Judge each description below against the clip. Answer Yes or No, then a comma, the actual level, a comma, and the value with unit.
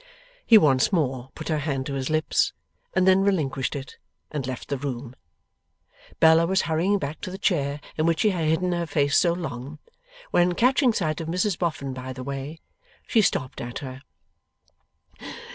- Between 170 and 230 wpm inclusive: Yes, average, 180 wpm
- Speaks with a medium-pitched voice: Yes, medium, 155 Hz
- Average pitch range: Yes, average, 4.7 semitones